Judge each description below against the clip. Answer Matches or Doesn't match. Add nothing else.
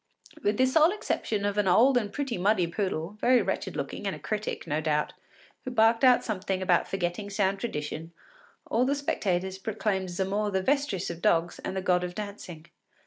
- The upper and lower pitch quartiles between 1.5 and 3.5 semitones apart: Doesn't match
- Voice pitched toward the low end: Doesn't match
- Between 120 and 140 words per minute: Doesn't match